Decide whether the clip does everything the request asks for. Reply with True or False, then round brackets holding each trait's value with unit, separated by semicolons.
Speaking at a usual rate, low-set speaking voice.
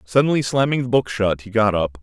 False (235 wpm; 115 Hz)